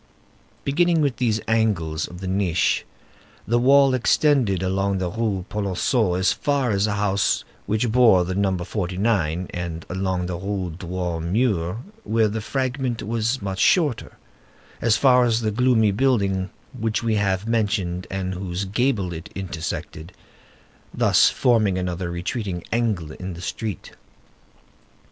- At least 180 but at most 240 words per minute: No, average, 140 wpm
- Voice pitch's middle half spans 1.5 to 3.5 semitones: No, average, 4.1 semitones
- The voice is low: Yes, low, 100 Hz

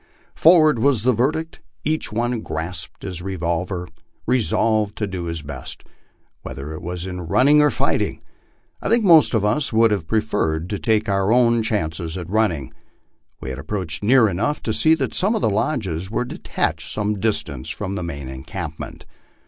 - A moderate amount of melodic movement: No, wide, 5.8 semitones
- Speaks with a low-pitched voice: Yes, low, 105 Hz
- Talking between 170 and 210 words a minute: Yes, average, 175 wpm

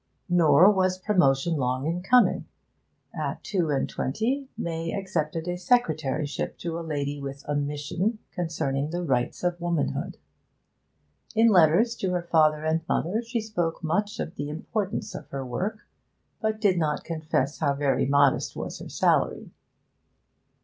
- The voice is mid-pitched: Yes, medium, 165 Hz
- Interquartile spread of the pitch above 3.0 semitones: Yes, average, 4.5 semitones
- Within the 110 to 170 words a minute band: Yes, average, 150 wpm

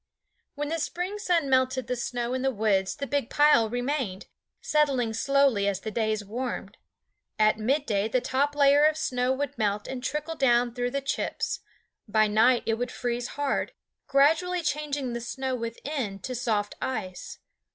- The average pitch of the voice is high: Yes, very high, 255 Hz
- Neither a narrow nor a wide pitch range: Yes, average, 4.2 semitones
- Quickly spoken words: No, average, 165 wpm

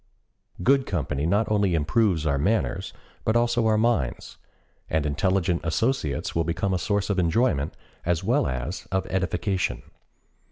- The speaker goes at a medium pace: Yes, average, 145 wpm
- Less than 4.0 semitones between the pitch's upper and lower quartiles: No, average, 5.2 semitones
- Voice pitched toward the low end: Yes, very low, 95 Hz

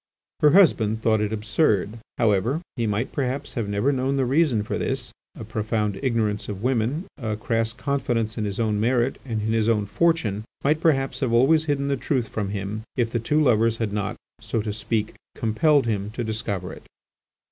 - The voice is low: Yes, low, 115 Hz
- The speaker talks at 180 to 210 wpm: Yes, average, 190 wpm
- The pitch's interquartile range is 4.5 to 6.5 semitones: No, average, 3.9 semitones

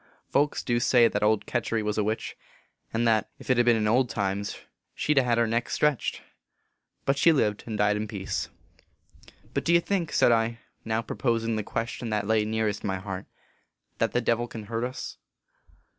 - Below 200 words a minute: No, fast, 205 wpm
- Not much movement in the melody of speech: Yes, narrow, 2.3 semitones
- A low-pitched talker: Yes, low, 115 Hz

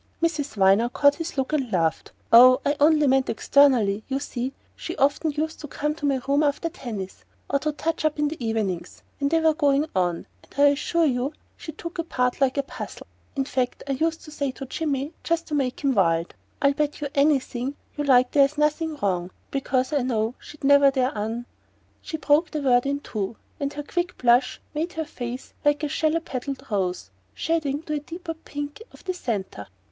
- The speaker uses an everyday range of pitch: Yes, average, 3.5 semitones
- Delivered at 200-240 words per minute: Yes, fast, 205 wpm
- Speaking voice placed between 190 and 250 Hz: No, very high, 280 Hz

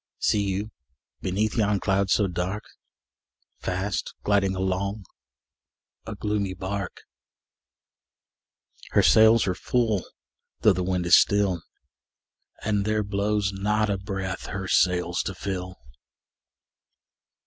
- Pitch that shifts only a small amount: Yes, narrow, 1.9 semitones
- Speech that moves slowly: Yes, slow, 110 wpm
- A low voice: Yes, low, 100 Hz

